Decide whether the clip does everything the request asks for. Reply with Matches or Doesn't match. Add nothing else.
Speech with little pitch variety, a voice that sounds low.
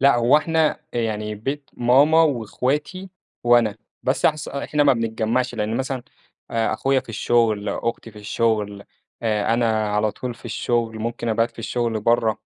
Doesn't match